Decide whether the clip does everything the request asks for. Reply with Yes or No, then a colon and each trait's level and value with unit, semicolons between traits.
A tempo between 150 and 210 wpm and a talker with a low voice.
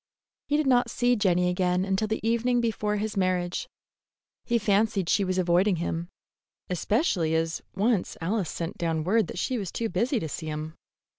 No: average, 175 wpm; high, 195 Hz